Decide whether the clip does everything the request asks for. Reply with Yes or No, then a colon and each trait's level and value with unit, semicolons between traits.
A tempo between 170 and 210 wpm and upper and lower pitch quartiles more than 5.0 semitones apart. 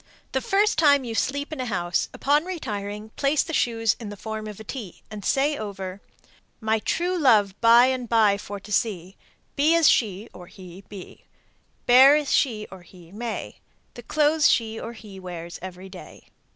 Yes: average, 185 wpm; wide, 5.6 semitones